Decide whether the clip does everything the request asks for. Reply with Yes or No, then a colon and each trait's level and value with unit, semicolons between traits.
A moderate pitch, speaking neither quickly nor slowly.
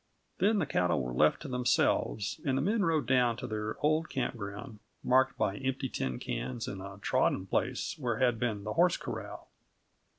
No: low, 120 Hz; average, 185 wpm